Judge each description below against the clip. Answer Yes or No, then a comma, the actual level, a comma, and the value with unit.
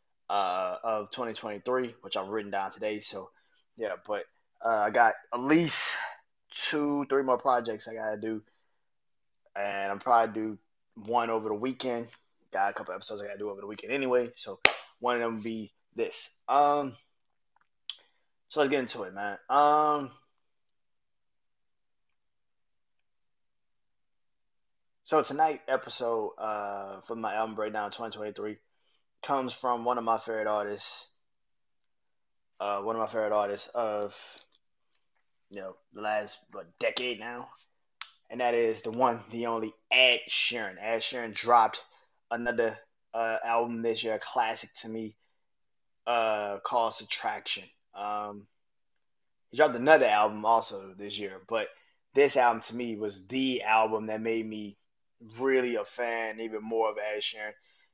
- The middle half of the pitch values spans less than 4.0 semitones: Yes, average, 2.7 semitones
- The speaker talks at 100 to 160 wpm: Yes, average, 145 wpm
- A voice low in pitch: Yes, low, 115 Hz